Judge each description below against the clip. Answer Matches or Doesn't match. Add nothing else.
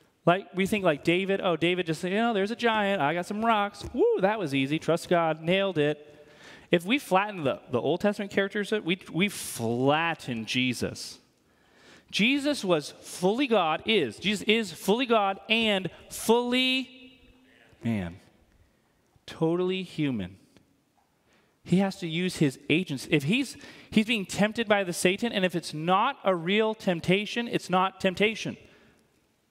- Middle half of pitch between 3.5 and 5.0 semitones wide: Matches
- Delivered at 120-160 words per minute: Matches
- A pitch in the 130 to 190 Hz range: Matches